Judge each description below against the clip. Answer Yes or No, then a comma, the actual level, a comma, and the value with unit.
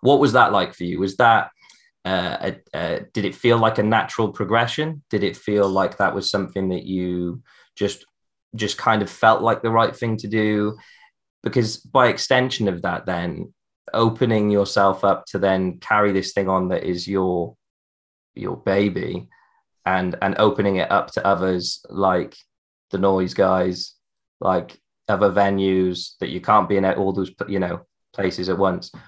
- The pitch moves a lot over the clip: No, average, 2.9 semitones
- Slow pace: No, average, 175 wpm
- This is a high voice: No, low, 100 Hz